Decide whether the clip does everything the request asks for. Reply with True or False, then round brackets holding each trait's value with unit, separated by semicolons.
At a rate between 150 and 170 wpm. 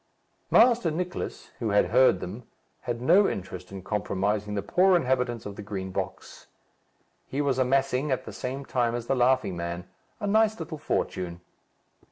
True (165 wpm)